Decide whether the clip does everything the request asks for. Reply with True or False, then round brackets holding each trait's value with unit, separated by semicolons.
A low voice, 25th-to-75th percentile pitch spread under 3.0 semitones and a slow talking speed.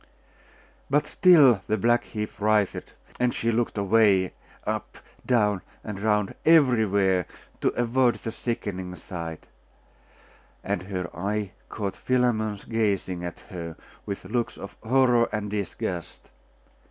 False (105 Hz; 3.6 semitones; 120 wpm)